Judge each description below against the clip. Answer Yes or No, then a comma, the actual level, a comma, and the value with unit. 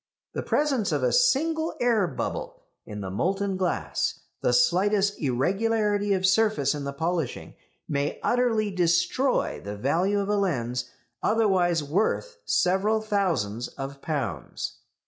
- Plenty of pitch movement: Yes, wide, 7.2 semitones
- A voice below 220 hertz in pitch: Yes, high, 190 Hz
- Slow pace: Yes, slow, 130 wpm